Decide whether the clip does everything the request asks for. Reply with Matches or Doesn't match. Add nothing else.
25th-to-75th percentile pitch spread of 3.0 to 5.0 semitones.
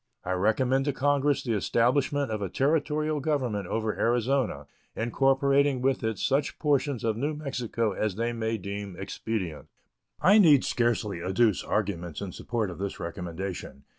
Doesn't match